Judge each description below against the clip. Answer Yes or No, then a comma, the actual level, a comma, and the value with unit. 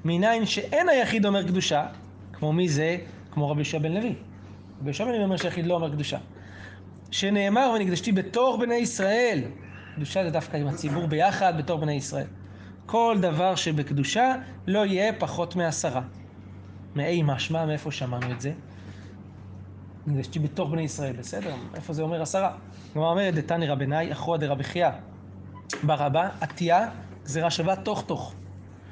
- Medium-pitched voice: Yes, medium, 155 Hz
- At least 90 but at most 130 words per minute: No, average, 145 wpm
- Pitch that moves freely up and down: Yes, wide, 7.0 semitones